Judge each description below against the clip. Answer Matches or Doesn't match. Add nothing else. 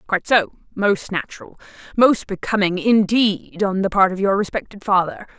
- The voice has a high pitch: Matches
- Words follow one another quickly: Doesn't match